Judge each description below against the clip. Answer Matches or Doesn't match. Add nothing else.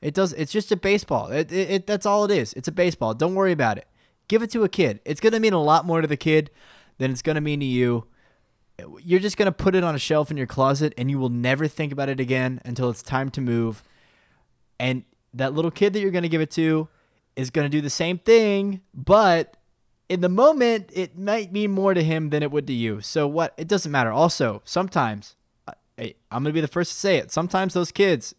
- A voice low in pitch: Doesn't match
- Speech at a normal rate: Doesn't match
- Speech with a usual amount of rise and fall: Doesn't match